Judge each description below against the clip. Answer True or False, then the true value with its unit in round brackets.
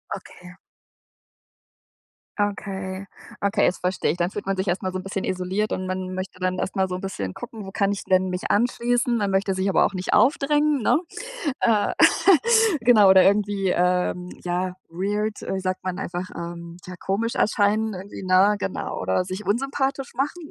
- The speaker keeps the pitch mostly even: True (2.3 semitones)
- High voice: True (195 Hz)